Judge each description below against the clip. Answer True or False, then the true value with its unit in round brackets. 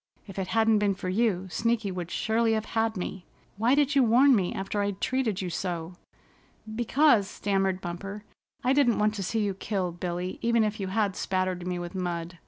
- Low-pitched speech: False (200 Hz)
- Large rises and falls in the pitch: False (3.5 semitones)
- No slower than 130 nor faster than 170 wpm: False (195 wpm)